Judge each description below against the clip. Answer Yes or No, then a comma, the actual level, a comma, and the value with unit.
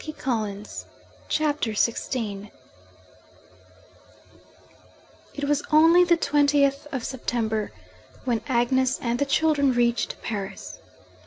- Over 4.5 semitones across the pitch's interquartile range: No, average, 4.2 semitones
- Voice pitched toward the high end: Yes, very high, 260 Hz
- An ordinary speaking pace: No, slow, 100 wpm